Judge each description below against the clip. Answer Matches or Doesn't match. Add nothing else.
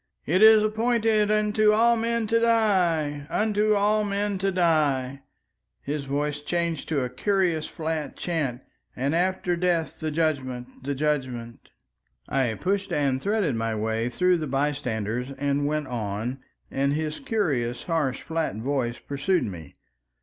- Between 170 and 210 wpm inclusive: Doesn't match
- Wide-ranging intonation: Matches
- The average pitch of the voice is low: Doesn't match